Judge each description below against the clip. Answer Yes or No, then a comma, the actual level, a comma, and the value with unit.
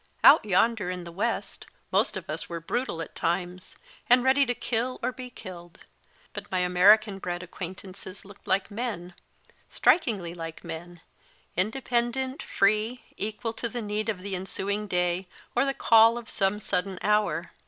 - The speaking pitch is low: No, high, 200 Hz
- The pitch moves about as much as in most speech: Yes, average, 4.5 semitones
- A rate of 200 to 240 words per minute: No, average, 165 wpm